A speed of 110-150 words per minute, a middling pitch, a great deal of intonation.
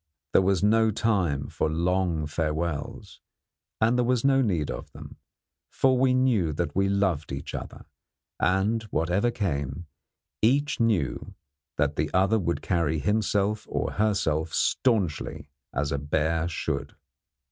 No: slow, 135 wpm; very low, 95 Hz; wide, 5.9 semitones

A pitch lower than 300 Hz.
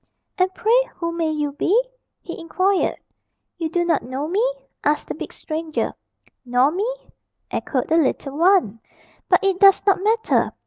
No: very high, 335 Hz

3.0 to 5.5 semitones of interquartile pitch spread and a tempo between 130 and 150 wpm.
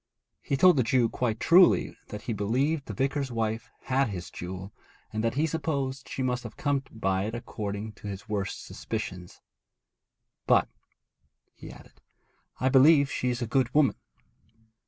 No: average, 4.4 semitones; average, 160 wpm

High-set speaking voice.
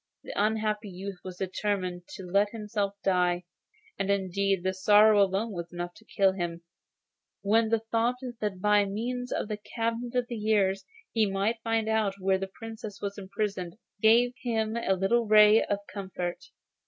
Yes: high, 205 Hz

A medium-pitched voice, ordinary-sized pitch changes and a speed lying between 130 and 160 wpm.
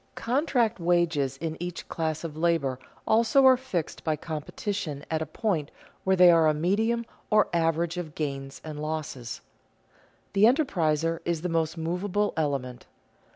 Yes: medium, 165 Hz; average, 4.3 semitones; average, 150 wpm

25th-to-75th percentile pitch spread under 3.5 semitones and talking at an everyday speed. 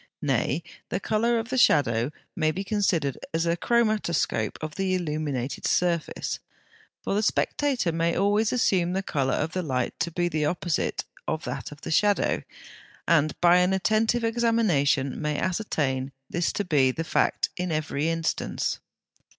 No: average, 5.1 semitones; average, 160 wpm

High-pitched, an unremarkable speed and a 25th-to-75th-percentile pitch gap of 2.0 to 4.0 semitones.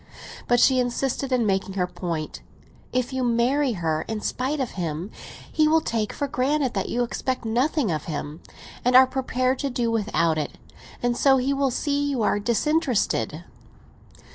No: high, 245 Hz; average, 175 wpm; average, 4.6 semitones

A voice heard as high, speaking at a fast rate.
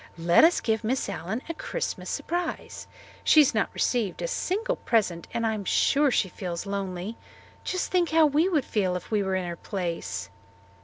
No: high, 220 Hz; average, 185 wpm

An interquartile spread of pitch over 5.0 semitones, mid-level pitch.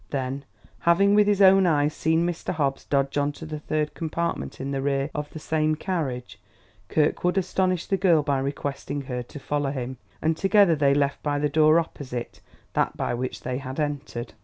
No: average, 3.3 semitones; medium, 150 Hz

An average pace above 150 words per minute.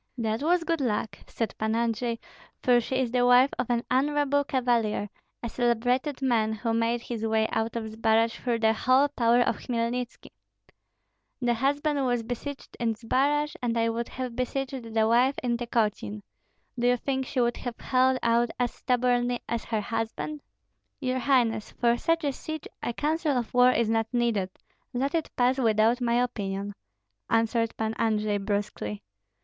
Yes: average, 170 wpm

